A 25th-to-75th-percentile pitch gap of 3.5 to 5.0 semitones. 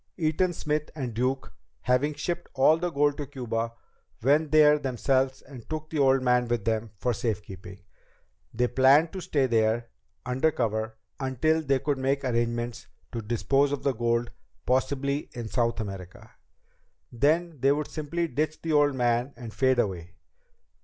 Yes: average, 3.8 semitones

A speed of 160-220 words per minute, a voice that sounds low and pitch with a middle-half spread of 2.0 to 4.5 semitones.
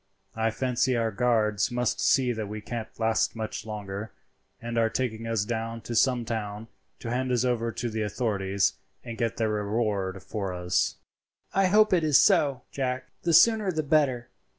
Yes: average, 175 wpm; low, 115 Hz; average, 2.9 semitones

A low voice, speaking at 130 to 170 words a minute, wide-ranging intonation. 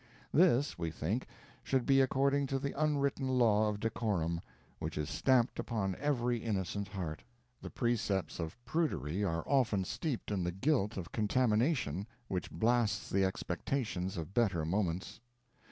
Yes: low, 105 Hz; average, 145 wpm; wide, 6.0 semitones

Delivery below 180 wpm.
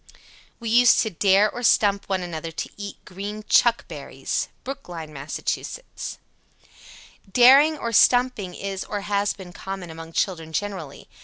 Yes: average, 145 wpm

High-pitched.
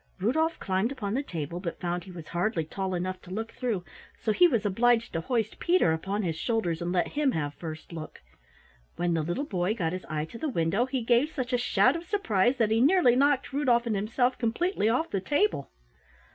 Yes: high, 215 Hz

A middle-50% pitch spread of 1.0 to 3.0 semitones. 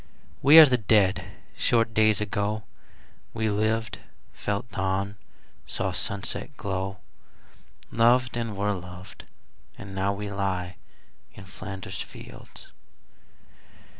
Yes: narrow, 2.6 semitones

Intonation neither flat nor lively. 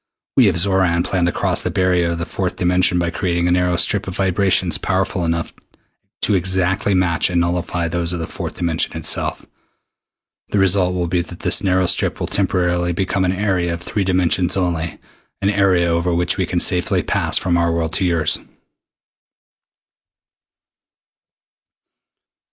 No: narrow, 1.6 semitones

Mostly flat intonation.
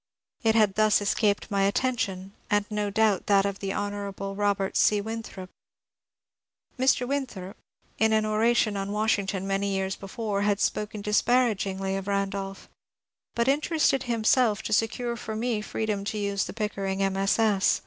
Yes: narrow, 2.1 semitones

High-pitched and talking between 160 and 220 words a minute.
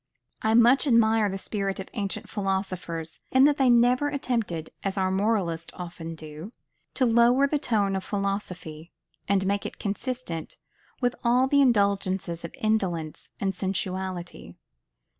No: high, 200 Hz; average, 145 wpm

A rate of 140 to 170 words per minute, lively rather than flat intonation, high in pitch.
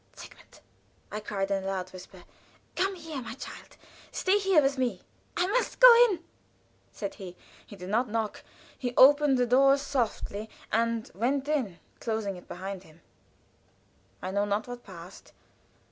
Yes: average, 160 wpm; wide, 6.3 semitones; high, 230 Hz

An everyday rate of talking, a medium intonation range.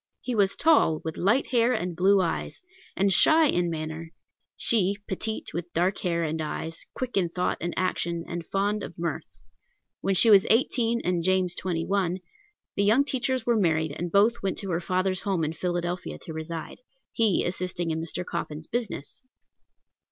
Yes: average, 175 wpm; average, 3.6 semitones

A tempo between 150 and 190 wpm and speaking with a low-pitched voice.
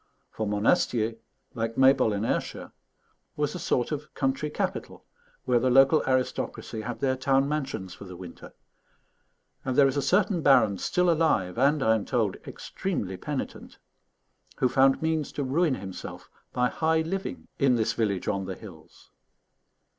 Yes: average, 155 wpm; low, 130 Hz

